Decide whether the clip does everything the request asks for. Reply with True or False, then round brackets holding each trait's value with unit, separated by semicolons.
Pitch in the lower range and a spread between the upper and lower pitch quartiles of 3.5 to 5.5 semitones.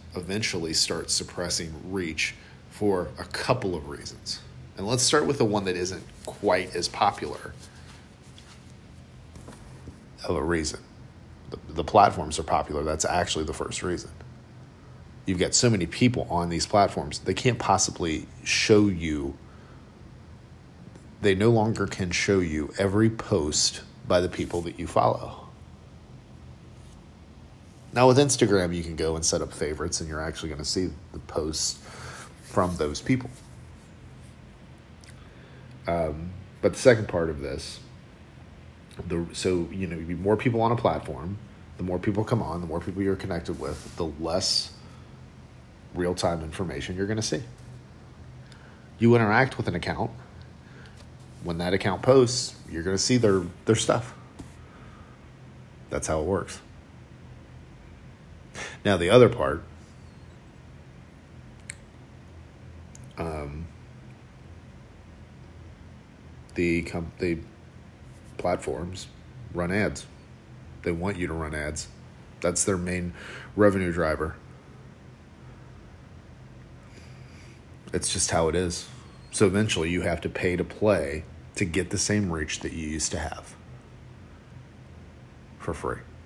True (90 Hz; 4.2 semitones)